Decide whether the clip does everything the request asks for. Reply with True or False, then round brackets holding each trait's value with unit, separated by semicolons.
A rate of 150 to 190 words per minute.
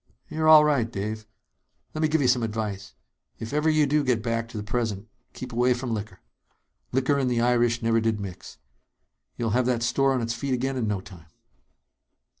False (200 wpm)